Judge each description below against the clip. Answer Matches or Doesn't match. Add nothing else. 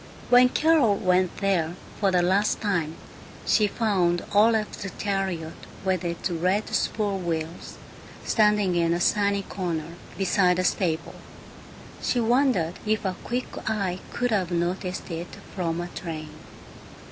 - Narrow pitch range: Doesn't match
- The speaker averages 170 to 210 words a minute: Doesn't match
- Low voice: Doesn't match